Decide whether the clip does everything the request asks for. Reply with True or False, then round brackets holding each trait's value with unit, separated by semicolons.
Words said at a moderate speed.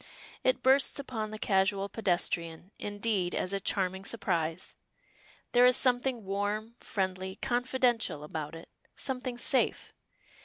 False (120 wpm)